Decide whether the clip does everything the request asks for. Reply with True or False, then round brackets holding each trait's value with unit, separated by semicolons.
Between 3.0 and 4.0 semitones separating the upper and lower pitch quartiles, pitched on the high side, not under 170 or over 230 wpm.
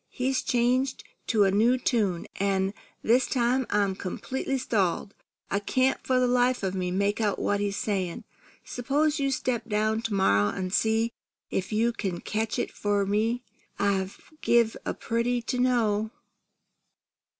False (3.7 semitones; 220 Hz; 155 wpm)